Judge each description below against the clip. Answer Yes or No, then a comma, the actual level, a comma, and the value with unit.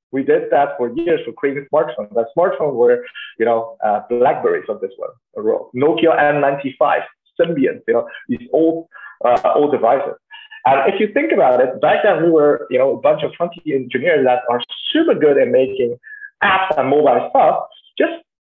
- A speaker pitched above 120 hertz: Yes, medium, 185 Hz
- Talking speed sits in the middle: Yes, average, 180 wpm